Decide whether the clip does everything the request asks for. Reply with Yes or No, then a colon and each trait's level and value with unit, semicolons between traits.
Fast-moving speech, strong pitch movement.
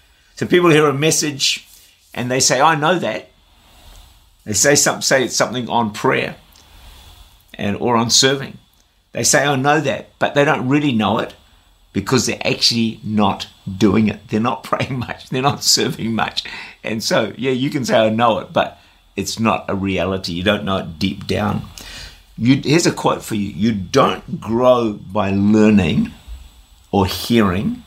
No: average, 175 wpm; wide, 5.9 semitones